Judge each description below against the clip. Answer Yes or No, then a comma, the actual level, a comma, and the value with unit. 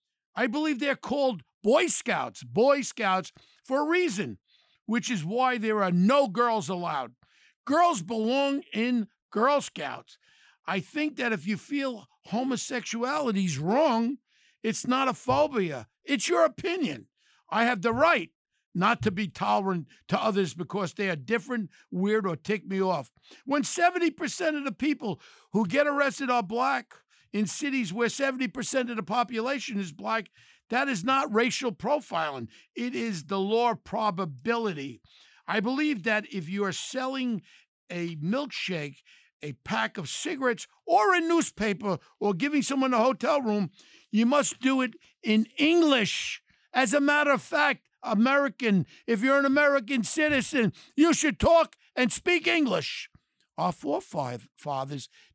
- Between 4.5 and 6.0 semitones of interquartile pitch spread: Yes, wide, 5.5 semitones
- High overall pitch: Yes, high, 240 Hz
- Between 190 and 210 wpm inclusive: No, average, 145 wpm